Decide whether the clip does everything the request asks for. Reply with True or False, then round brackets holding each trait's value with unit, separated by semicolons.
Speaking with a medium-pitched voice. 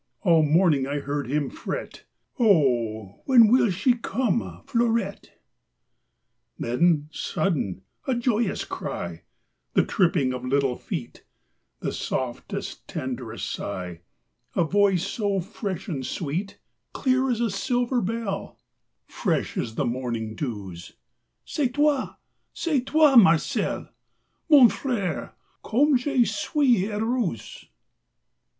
False (195 Hz)